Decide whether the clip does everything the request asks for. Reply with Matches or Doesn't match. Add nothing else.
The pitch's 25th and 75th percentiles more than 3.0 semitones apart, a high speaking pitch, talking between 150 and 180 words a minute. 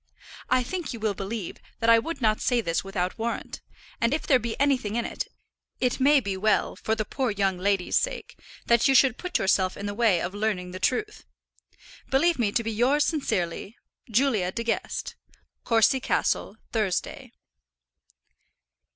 Matches